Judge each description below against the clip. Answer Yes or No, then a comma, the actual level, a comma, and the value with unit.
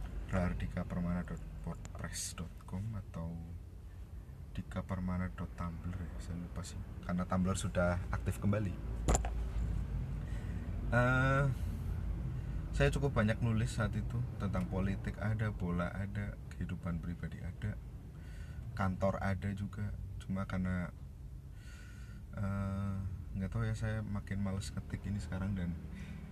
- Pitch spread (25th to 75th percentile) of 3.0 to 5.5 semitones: No, narrow, 2.6 semitones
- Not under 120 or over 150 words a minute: No, average, 100 wpm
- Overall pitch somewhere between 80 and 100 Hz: Yes, very low, 95 Hz